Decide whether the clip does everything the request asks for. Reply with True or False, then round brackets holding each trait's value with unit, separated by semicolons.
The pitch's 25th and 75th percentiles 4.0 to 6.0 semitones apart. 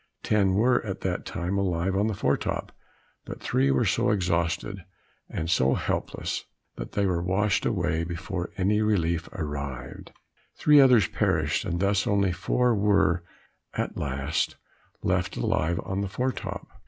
False (3.3 semitones)